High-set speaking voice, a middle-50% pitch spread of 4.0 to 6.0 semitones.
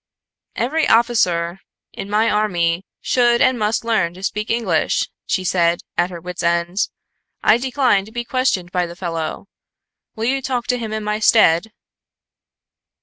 Yes: high, 210 Hz; average, 5.2 semitones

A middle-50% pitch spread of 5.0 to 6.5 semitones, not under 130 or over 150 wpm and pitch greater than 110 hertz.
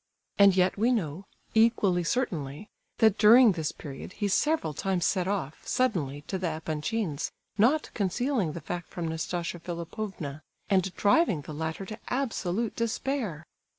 Yes: wide, 5.5 semitones; average, 145 wpm; high, 190 Hz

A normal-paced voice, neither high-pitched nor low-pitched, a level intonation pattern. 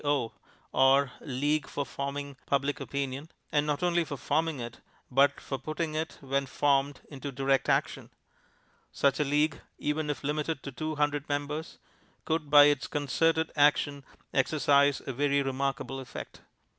Yes: average, 150 wpm; medium, 145 Hz; narrow, 1.5 semitones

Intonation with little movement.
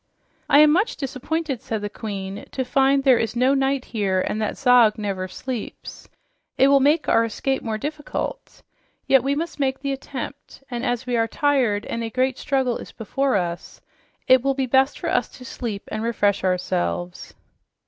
No: average, 4.0 semitones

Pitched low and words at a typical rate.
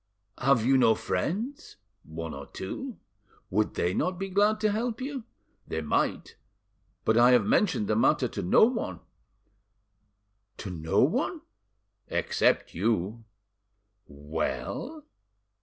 No: low, 115 Hz; slow, 125 wpm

